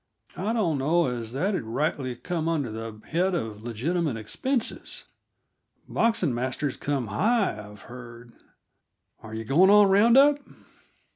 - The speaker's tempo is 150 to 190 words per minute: No, slow, 135 wpm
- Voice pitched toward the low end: No, medium, 145 Hz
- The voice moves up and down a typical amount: No, wide, 8.4 semitones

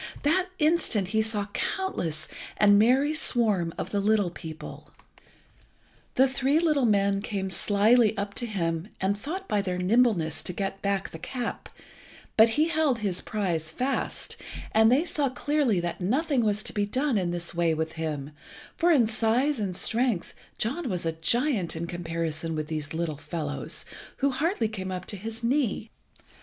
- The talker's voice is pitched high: Yes, high, 210 Hz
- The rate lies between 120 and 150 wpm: No, average, 170 wpm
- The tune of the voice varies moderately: No, wide, 6.7 semitones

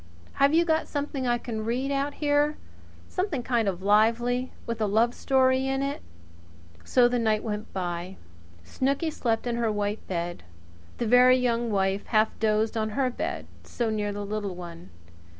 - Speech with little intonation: No, average, 3.9 semitones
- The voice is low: No, high, 235 Hz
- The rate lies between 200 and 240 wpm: No, average, 175 wpm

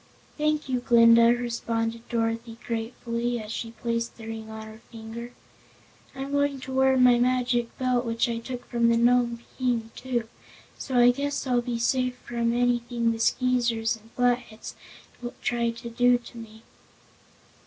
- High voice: Yes, high, 235 Hz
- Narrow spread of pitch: Yes, narrow, 1.3 semitones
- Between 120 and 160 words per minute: Yes, average, 155 wpm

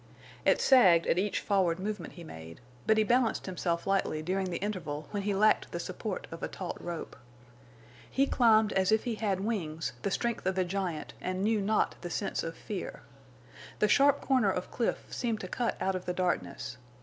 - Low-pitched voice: No, high, 195 Hz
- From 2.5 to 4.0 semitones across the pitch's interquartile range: Yes, average, 3.6 semitones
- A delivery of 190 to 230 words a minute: Yes, average, 195 wpm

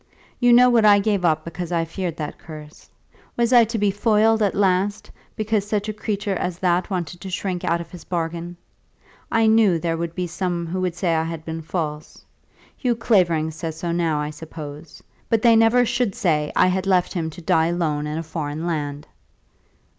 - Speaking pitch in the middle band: Yes, medium, 175 Hz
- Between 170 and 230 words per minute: Yes, average, 200 wpm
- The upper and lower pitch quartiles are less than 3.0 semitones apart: No, average, 4.2 semitones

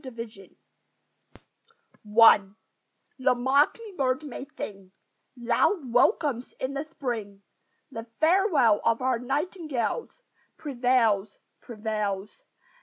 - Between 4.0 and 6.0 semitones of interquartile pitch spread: Yes, average, 4.4 semitones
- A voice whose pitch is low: No, high, 245 Hz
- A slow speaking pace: Yes, slow, 95 wpm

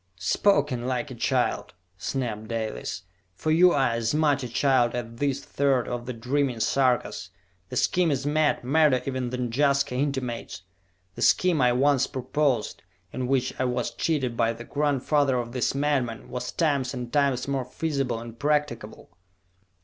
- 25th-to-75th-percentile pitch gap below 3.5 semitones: Yes, average, 2.9 semitones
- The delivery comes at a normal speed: Yes, average, 160 wpm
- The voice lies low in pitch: Yes, low, 130 Hz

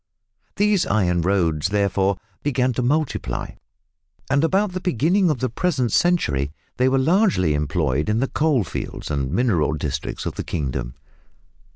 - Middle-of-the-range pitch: No, low, 110 Hz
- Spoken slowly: No, average, 150 wpm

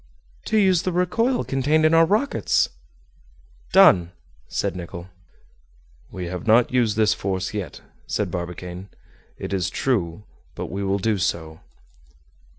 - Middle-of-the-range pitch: No, low, 105 Hz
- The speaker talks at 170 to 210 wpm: No, slow, 135 wpm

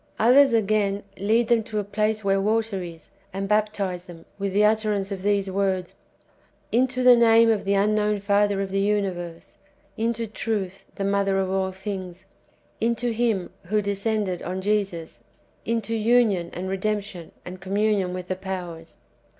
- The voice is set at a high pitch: Yes, high, 200 Hz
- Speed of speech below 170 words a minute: No, average, 175 wpm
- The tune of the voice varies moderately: No, narrow, 2.3 semitones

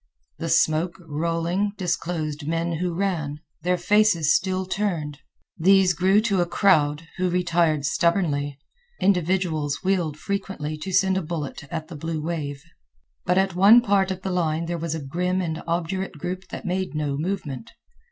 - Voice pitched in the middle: Yes, medium, 170 Hz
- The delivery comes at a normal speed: Yes, average, 160 wpm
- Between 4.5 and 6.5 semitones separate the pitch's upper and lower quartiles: No, average, 3.4 semitones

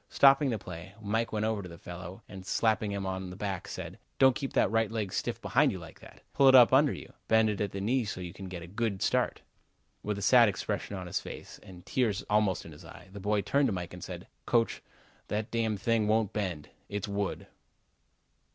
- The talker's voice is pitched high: No, low, 105 Hz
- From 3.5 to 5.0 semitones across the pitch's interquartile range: No, average, 3.1 semitones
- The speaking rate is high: Yes, fast, 230 wpm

